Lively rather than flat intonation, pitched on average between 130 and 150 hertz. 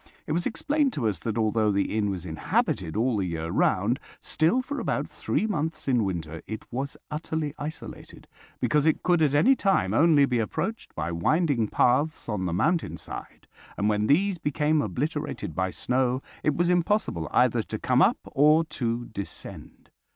Yes: wide, 7.4 semitones; low, 135 Hz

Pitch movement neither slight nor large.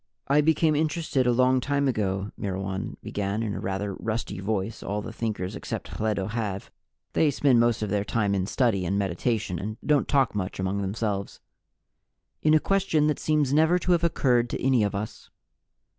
No: wide, 6.0 semitones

